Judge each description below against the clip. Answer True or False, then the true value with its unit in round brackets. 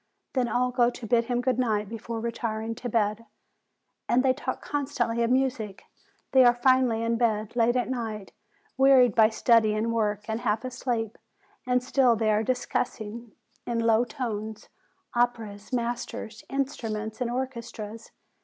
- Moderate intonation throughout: False (2.3 semitones)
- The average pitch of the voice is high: True (235 Hz)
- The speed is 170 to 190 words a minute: False (155 wpm)